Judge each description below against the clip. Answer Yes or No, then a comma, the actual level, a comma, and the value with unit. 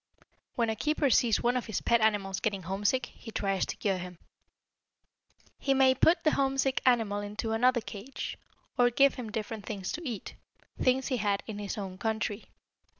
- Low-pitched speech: No, high, 225 Hz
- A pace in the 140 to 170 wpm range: No, average, 180 wpm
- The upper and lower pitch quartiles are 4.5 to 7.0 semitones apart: No, average, 3.9 semitones